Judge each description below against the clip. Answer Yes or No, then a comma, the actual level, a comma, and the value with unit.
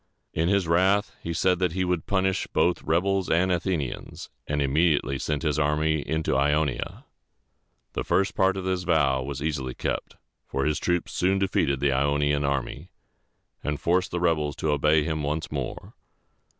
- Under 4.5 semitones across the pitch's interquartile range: Yes, average, 3.7 semitones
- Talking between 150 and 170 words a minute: Yes, average, 165 wpm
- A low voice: Yes, very low, 80 Hz